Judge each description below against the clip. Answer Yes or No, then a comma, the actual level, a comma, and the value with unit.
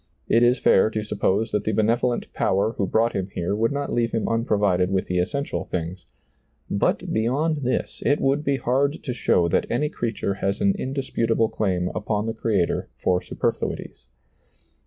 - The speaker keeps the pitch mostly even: No, average, 4.4 semitones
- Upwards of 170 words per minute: Yes, average, 180 wpm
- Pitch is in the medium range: No, low, 110 Hz